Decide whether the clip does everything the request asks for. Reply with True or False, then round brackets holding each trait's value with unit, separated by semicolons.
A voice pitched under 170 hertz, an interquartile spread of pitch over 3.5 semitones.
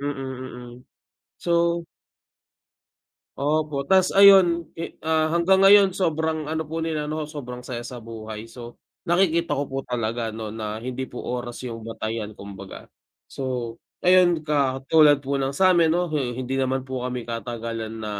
True (135 Hz; 5.2 semitones)